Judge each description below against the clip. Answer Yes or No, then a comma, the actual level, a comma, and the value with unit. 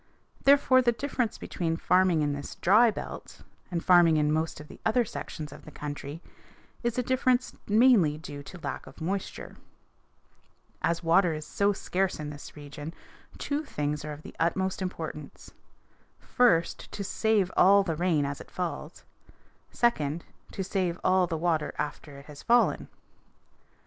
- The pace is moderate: Yes, average, 160 wpm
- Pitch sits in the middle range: Yes, medium, 175 Hz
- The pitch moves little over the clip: No, average, 5.1 semitones